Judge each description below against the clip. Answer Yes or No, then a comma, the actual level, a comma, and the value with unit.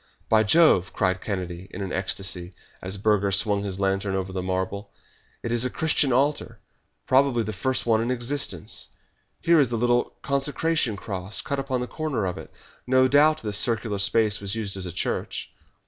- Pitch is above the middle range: No, low, 110 Hz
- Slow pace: No, average, 180 wpm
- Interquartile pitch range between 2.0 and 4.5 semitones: No, average, 5.0 semitones